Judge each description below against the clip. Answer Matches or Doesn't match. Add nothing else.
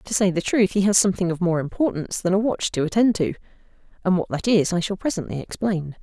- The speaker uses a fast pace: Matches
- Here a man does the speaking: Doesn't match